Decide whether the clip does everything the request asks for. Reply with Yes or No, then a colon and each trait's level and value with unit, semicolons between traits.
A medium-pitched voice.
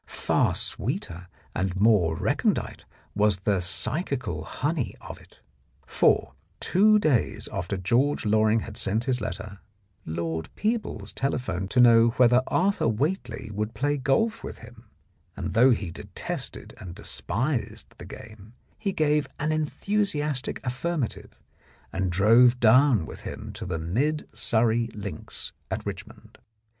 No: low, 115 Hz